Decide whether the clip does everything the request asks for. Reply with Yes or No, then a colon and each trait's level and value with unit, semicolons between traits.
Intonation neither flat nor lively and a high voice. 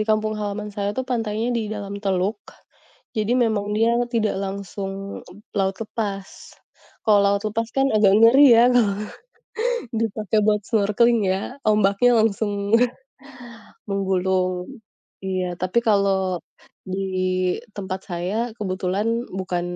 No: narrow, 2.2 semitones; high, 200 Hz